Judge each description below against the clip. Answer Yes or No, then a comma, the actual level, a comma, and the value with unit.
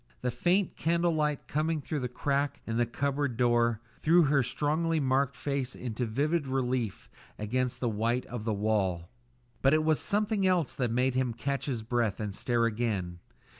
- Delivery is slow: No, average, 175 wpm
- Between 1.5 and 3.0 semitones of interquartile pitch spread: No, average, 4.3 semitones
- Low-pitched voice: Yes, low, 130 Hz